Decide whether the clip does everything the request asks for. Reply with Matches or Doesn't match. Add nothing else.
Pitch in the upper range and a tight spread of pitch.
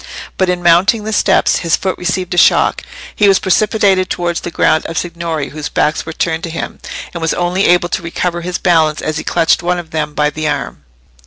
Doesn't match